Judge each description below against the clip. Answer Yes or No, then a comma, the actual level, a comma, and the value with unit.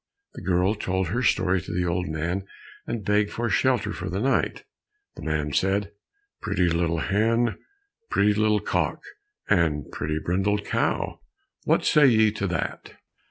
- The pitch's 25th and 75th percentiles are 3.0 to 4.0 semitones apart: Yes, average, 3.6 semitones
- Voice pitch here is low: Yes, very low, 95 Hz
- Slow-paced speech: No, average, 155 wpm